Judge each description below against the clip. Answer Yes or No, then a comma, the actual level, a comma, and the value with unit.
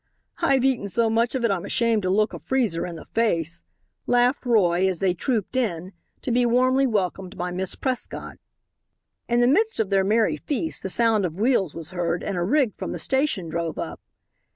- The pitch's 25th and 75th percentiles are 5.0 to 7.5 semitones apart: Yes, wide, 5.4 semitones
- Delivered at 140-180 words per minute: No, average, 200 wpm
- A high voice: Yes, high, 215 Hz